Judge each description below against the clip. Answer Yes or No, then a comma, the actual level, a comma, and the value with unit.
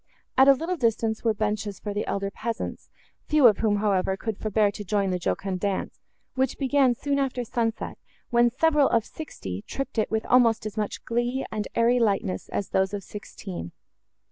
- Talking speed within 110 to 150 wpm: No, average, 185 wpm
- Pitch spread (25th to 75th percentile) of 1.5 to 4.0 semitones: Yes, average, 3.5 semitones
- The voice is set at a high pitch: Yes, high, 220 Hz